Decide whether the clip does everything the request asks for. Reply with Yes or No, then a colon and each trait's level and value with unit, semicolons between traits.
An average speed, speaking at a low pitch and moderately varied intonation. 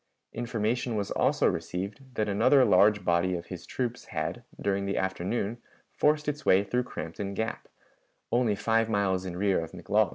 Yes: average, 165 wpm; low, 105 Hz; average, 4.0 semitones